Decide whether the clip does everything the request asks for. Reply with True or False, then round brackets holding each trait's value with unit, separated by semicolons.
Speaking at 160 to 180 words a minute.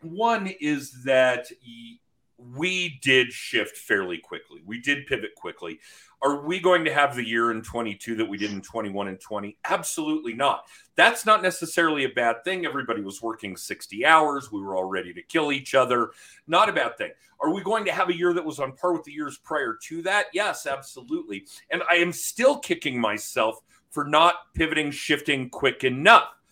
False (190 wpm)